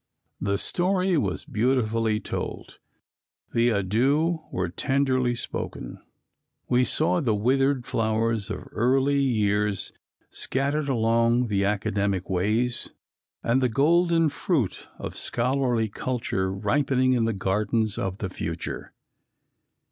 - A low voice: Yes, low, 115 Hz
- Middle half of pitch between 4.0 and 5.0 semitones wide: Yes, average, 4.4 semitones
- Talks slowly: Yes, slow, 110 wpm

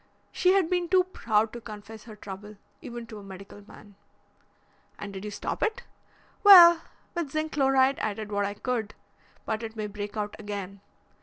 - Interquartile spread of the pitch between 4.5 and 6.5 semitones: Yes, average, 5.2 semitones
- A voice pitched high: Yes, high, 220 Hz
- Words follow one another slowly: No, average, 180 wpm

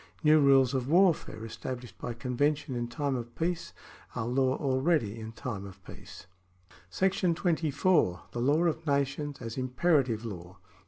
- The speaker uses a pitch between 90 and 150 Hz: Yes, low, 135 Hz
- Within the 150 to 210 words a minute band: Yes, average, 155 wpm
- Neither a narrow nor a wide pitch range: Yes, average, 4.5 semitones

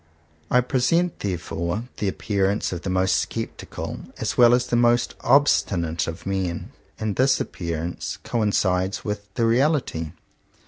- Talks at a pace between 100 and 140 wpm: Yes, slow, 135 wpm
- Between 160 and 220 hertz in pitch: No, low, 105 Hz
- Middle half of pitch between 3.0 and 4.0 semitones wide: No, average, 5.1 semitones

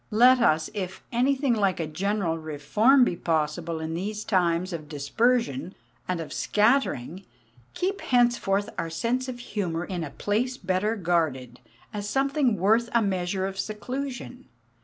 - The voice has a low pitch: No, high, 195 Hz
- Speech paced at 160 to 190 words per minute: No, average, 145 wpm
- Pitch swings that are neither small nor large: No, wide, 6.2 semitones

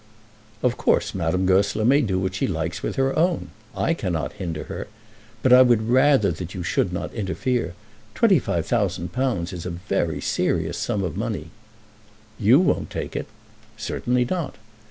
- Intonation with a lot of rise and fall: Yes, wide, 6.2 semitones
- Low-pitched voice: Yes, low, 100 Hz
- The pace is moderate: Yes, average, 170 wpm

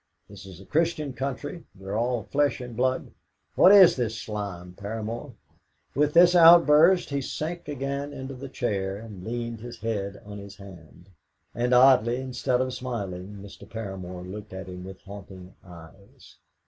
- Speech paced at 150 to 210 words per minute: Yes, average, 160 wpm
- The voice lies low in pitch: Yes, low, 115 Hz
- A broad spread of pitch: Yes, wide, 5.7 semitones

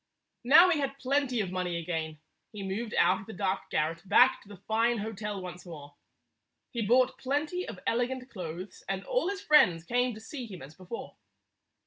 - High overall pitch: Yes, high, 215 Hz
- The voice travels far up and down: Yes, wide, 5.9 semitones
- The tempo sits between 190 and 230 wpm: Yes, average, 195 wpm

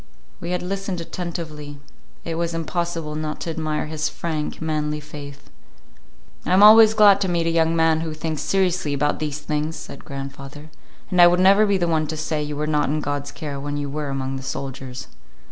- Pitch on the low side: No, medium, 155 Hz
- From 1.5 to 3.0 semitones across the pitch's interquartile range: Yes, narrow, 2.6 semitones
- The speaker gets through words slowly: No, average, 200 wpm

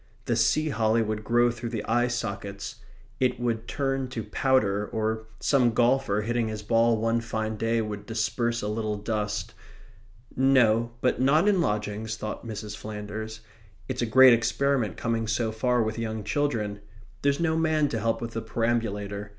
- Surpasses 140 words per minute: Yes, average, 165 wpm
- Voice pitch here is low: Yes, low, 115 Hz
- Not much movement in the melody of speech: Yes, narrow, 2.1 semitones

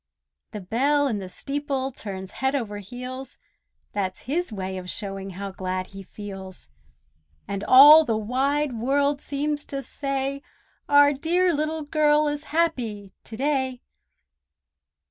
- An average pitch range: No, wide, 6.3 semitones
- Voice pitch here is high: Yes, very high, 265 Hz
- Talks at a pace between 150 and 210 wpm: No, slow, 135 wpm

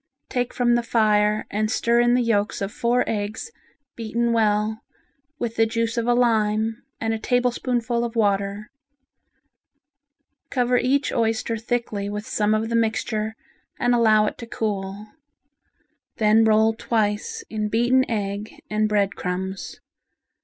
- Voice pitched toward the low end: No, high, 220 Hz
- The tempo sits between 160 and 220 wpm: No, average, 140 wpm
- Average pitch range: No, narrow, 2.0 semitones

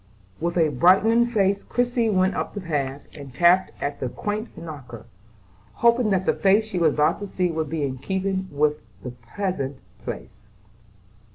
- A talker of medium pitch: Yes, medium, 180 Hz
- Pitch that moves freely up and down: Yes, wide, 5.7 semitones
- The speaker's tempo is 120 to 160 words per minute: No, average, 170 wpm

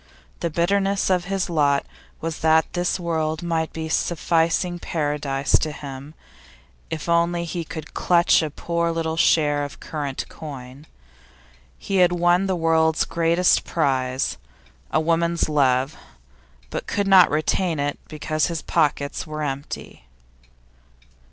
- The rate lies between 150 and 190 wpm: No, slow, 135 wpm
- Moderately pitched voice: Yes, medium, 160 Hz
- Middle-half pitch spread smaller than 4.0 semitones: Yes, narrow, 2.6 semitones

